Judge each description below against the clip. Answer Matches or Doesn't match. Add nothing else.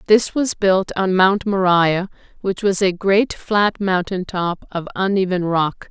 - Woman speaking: Matches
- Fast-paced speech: Doesn't match